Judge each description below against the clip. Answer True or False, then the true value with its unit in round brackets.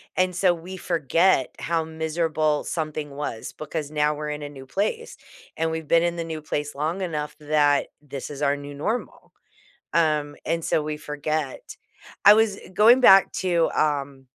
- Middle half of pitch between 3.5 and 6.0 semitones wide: False (2.6 semitones)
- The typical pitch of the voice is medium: True (155 Hz)